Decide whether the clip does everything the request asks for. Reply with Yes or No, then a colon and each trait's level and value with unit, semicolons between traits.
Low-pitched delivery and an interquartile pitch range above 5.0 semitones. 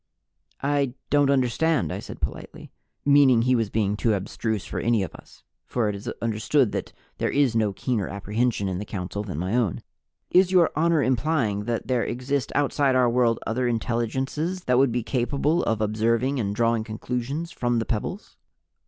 No: low, 120 Hz; average, 4.1 semitones